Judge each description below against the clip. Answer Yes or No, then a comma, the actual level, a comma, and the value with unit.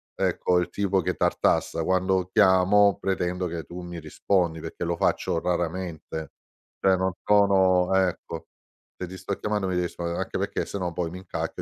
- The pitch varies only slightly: Yes, narrow, 1.5 semitones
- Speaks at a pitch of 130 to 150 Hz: No, very low, 90 Hz